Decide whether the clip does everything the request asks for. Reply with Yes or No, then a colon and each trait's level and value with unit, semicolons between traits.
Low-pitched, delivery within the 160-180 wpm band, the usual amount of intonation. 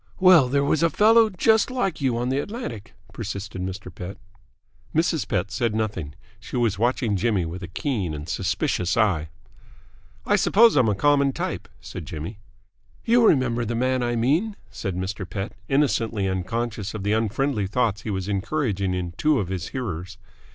No: low, 115 Hz; average, 170 wpm; wide, 6.5 semitones